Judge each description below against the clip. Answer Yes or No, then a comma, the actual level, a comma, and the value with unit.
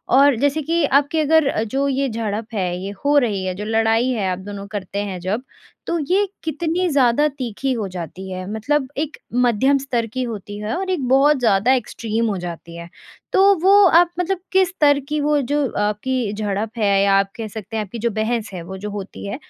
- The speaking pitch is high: Yes, high, 230 Hz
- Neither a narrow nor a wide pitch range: No, wide, 5.9 semitones